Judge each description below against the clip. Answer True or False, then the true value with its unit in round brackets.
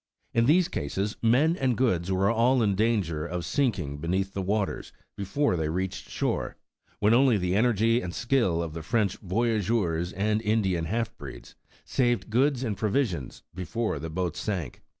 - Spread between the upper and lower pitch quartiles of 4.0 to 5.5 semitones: True (4.7 semitones)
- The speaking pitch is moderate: False (105 Hz)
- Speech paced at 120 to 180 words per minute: True (170 wpm)